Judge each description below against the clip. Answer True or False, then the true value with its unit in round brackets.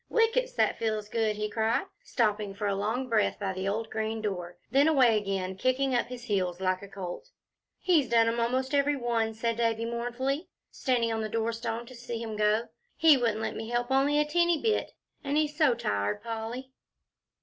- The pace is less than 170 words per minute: False (195 wpm)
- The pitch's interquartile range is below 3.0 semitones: False (3.7 semitones)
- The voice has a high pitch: True (230 Hz)